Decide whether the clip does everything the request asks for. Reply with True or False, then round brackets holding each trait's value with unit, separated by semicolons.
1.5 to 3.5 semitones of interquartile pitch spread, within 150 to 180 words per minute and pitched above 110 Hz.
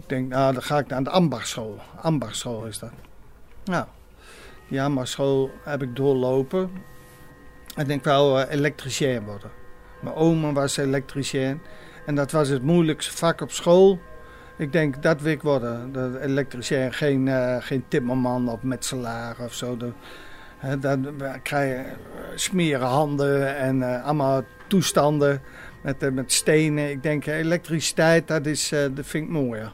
True (2.9 semitones; 155 wpm; 140 Hz)